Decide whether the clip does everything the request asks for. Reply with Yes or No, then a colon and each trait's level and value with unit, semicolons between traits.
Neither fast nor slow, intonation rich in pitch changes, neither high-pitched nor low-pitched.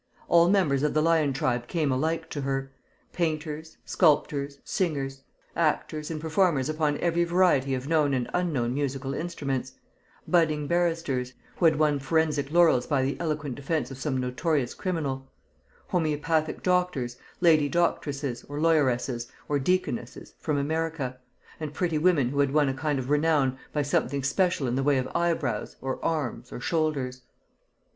No: average, 155 wpm; average, 3.4 semitones; medium, 150 Hz